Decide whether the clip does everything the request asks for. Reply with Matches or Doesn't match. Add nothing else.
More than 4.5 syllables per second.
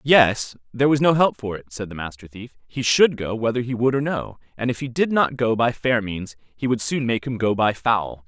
Matches